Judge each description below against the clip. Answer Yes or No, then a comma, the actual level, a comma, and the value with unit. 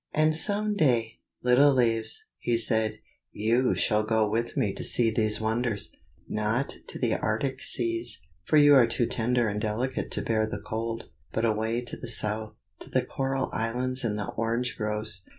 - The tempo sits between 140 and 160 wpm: No, average, 175 wpm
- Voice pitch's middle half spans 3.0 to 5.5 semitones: No, narrow, 2.4 semitones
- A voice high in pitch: No, low, 115 Hz